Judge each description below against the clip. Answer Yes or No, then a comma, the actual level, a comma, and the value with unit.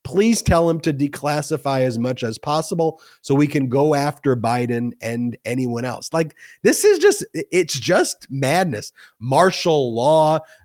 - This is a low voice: No, medium, 145 Hz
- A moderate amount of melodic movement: Yes, average, 4.4 semitones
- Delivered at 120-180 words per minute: Yes, average, 150 wpm